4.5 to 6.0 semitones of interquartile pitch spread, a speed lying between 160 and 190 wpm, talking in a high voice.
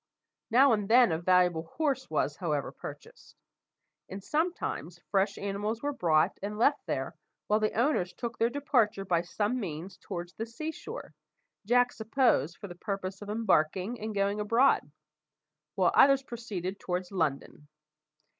No: average, 5.0 semitones; average, 150 wpm; high, 205 Hz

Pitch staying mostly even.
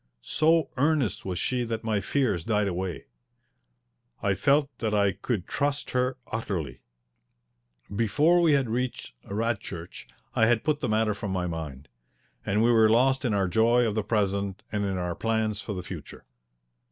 No: average, 4.1 semitones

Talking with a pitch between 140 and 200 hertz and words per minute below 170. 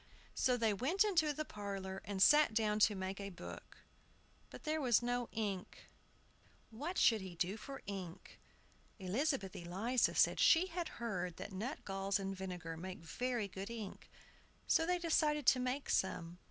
No: high, 215 Hz; average, 160 wpm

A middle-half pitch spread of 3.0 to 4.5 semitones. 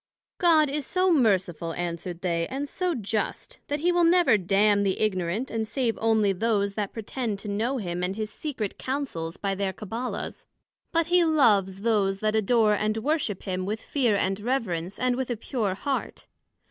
No: average, 5.3 semitones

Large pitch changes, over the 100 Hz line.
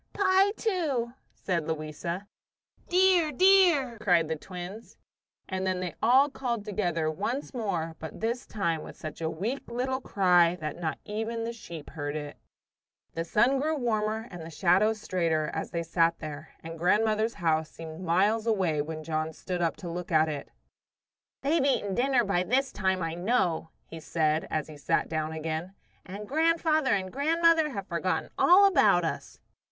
Yes: wide, 6.9 semitones; high, 190 Hz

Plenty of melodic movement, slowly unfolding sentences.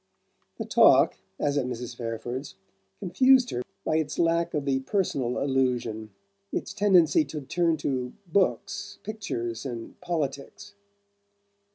Yes: wide, 6.1 semitones; slow, 125 wpm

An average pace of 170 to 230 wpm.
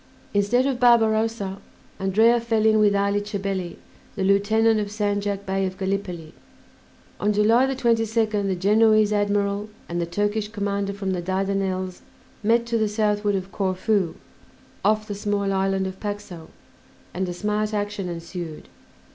No: average, 145 wpm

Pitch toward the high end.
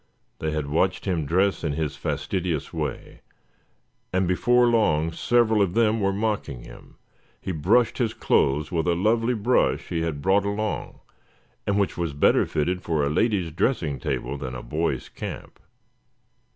No: very low, 90 Hz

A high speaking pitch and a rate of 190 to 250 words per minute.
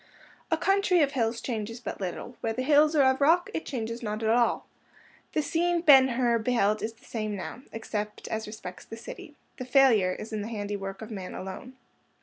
Yes: high, 230 Hz; average, 200 wpm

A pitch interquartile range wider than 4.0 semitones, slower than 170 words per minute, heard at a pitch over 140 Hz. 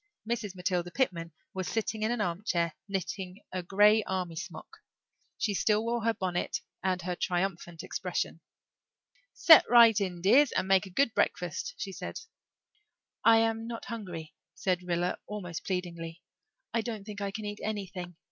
No: average, 3.7 semitones; average, 155 wpm; high, 190 Hz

